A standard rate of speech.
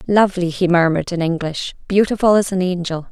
Yes: average, 175 wpm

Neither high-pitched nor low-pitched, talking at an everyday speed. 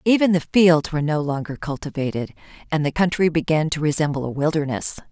Yes: medium, 155 Hz; average, 175 wpm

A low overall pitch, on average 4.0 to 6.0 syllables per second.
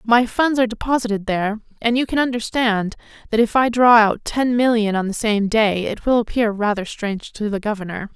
No: high, 225 Hz; 5.5 syllables/s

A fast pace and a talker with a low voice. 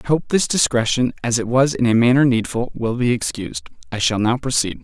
Yes: fast, 225 wpm; low, 125 Hz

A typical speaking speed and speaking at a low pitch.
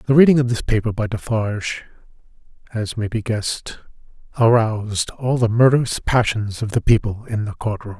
Yes: average, 175 wpm; low, 110 Hz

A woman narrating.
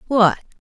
Yes: female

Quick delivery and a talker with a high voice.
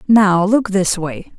No: average, 175 wpm; high, 195 Hz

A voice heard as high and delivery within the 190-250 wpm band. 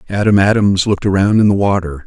No: low, 100 Hz; fast, 205 wpm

